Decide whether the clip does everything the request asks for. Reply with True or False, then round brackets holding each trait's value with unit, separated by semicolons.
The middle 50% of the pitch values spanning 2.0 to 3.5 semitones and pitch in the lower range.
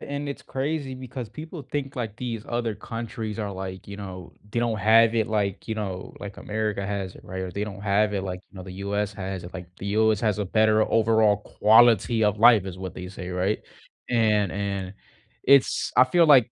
True (2.9 semitones; 105 Hz)